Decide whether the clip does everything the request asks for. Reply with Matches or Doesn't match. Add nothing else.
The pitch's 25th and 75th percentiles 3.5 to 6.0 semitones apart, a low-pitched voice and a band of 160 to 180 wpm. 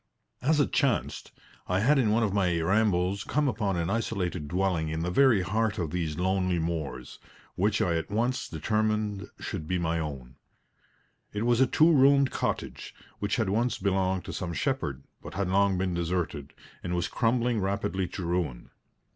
Matches